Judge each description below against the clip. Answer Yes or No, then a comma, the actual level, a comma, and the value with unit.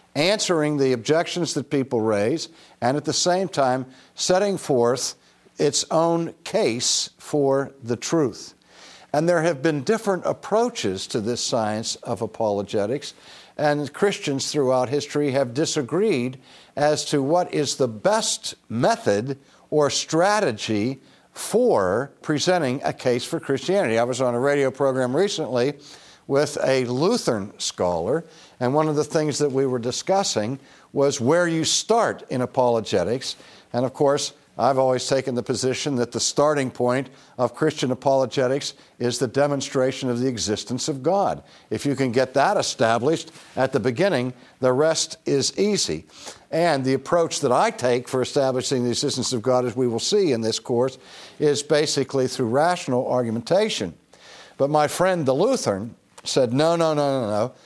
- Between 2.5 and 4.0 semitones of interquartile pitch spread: Yes, average, 3.4 semitones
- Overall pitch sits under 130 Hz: No, low, 135 Hz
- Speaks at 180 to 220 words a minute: No, average, 155 wpm